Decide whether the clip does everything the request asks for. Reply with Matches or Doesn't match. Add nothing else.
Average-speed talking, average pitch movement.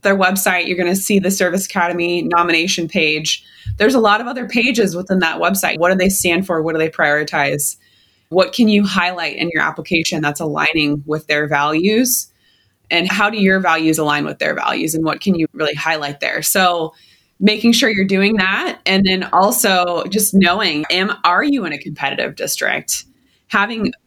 Matches